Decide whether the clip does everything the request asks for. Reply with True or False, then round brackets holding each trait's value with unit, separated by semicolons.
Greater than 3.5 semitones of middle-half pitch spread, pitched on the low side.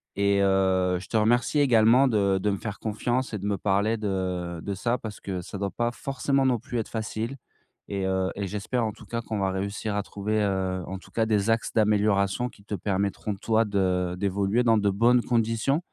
False (2.9 semitones; 105 Hz)